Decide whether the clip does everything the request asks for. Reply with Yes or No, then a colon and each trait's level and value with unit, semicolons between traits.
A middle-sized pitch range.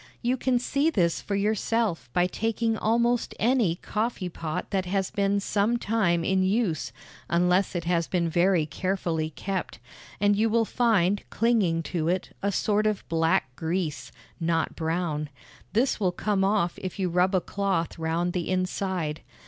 Yes: average, 3.9 semitones